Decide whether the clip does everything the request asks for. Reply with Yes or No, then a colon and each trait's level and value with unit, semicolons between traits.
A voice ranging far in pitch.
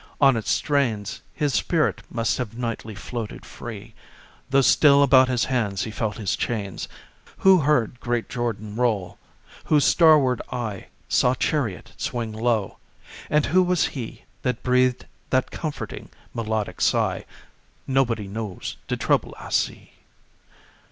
No: average, 3.8 semitones